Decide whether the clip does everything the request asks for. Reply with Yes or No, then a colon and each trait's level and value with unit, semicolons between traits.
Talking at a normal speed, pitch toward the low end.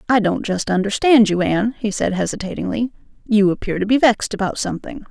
No: average, 190 wpm; high, 215 Hz